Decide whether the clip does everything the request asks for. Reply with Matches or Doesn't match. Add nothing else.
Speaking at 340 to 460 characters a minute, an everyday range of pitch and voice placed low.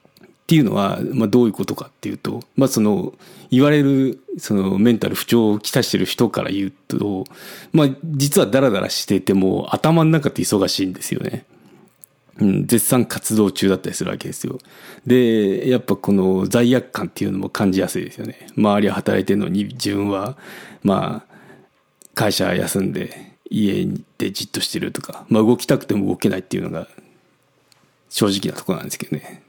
Matches